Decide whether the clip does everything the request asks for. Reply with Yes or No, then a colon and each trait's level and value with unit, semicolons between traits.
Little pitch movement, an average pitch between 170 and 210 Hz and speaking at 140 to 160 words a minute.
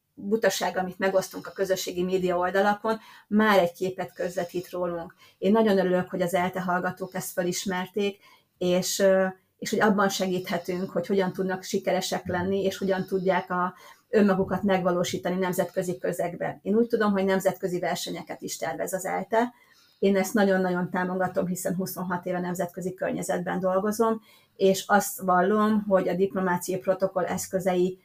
Yes: narrow, 1.2 semitones; medium, 185 Hz; average, 145 wpm